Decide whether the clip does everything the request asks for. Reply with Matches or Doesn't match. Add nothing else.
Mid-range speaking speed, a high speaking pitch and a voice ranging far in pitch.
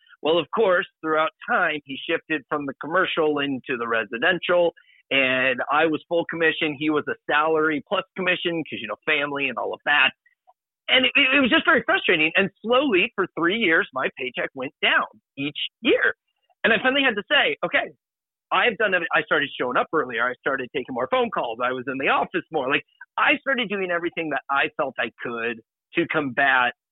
Doesn't match